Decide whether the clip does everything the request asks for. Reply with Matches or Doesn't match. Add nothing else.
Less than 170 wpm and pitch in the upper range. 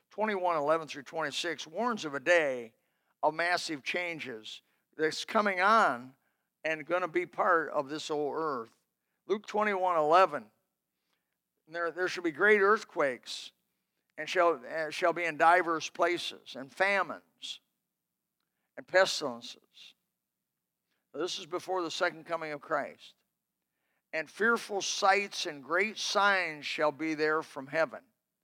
Doesn't match